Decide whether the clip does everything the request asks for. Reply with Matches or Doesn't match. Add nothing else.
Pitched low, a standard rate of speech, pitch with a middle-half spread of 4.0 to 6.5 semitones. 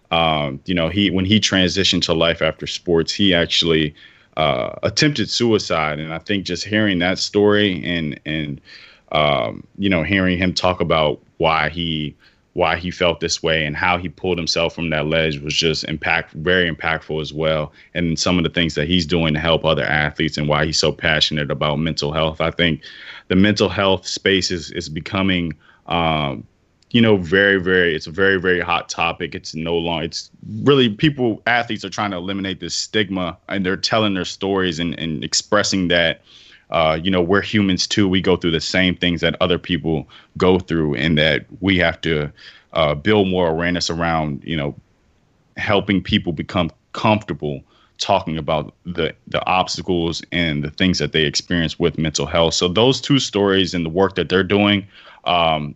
Doesn't match